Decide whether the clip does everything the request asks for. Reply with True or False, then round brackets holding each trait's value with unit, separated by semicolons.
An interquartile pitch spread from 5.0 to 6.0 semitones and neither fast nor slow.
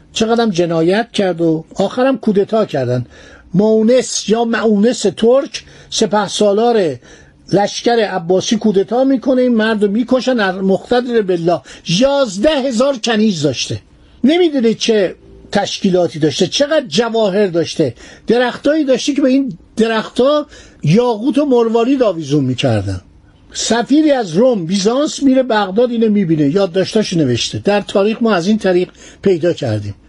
True (5.4 semitones; 125 wpm)